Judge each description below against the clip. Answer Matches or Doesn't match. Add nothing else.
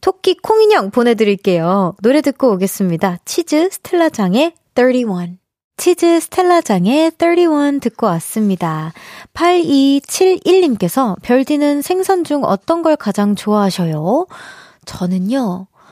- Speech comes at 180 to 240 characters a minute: Matches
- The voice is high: Matches